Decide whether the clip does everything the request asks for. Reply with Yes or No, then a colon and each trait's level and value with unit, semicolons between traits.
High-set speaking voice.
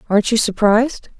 Yes: high, 220 Hz